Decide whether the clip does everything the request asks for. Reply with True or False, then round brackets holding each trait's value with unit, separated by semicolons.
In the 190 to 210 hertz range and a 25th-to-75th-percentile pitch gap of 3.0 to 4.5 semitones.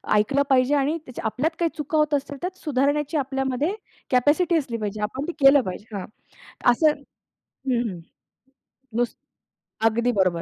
False (270 Hz; 4.2 semitones)